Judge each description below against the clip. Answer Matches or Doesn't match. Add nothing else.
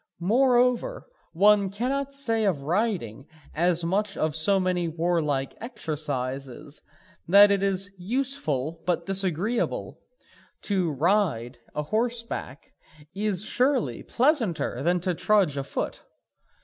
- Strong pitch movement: Matches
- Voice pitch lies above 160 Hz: Matches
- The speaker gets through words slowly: Matches